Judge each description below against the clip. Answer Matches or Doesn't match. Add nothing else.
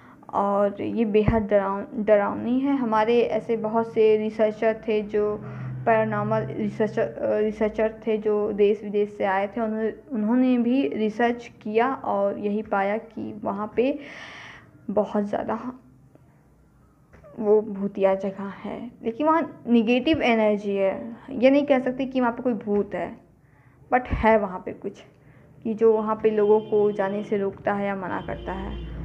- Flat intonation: Matches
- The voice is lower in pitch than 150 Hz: Doesn't match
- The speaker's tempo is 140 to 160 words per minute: Matches